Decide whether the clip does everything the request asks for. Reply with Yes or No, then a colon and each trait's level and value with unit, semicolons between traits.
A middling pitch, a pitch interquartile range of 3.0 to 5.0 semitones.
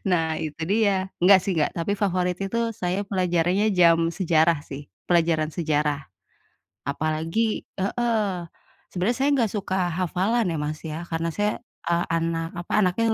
Yes: medium, 180 Hz; average, 3.5 semitones